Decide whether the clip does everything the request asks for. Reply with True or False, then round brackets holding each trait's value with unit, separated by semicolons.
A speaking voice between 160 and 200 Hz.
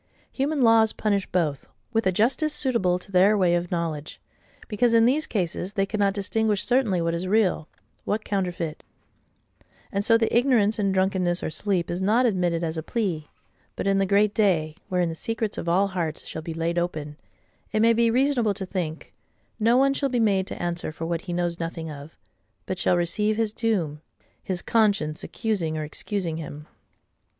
True (190 Hz)